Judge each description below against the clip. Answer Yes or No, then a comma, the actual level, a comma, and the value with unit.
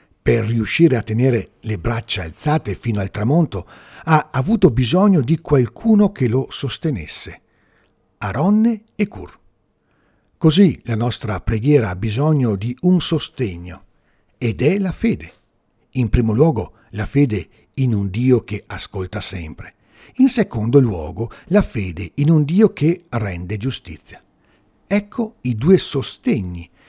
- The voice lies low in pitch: Yes, low, 120 Hz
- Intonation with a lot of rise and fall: Yes, wide, 7.1 semitones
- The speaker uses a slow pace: No, average, 135 wpm